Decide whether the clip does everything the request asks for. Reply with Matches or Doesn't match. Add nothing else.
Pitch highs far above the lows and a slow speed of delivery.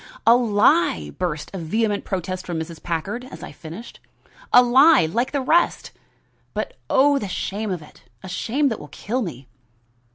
Doesn't match